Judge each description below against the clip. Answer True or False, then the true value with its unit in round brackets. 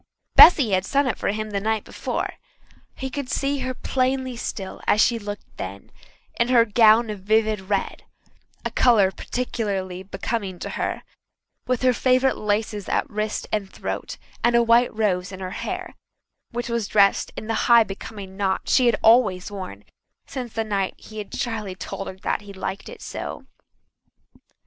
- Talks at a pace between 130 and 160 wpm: False (175 wpm)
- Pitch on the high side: True (215 Hz)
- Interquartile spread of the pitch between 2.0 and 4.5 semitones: True (3.5 semitones)